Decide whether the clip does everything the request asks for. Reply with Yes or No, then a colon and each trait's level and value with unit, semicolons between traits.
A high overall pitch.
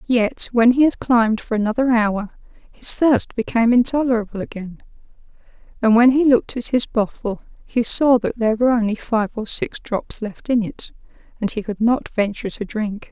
Yes: high, 230 Hz